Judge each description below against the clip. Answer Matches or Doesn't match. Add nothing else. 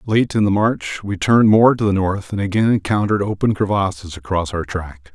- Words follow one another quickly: Matches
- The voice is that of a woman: Doesn't match